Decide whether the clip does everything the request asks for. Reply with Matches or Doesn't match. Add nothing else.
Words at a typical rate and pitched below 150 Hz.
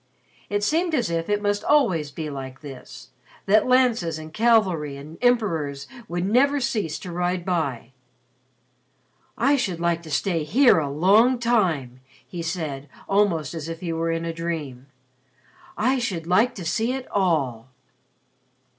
Doesn't match